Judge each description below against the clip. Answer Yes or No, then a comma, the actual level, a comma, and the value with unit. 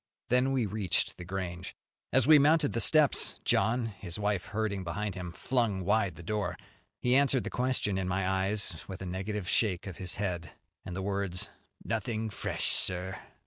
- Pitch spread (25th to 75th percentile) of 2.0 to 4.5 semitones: Yes, average, 3.5 semitones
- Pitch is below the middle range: Yes, low, 100 Hz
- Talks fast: No, average, 180 wpm